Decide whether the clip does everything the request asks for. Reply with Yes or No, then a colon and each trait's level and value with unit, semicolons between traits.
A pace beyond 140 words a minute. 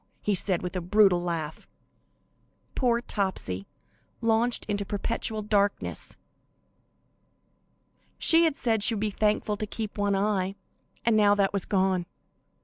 No: slow, 135 wpm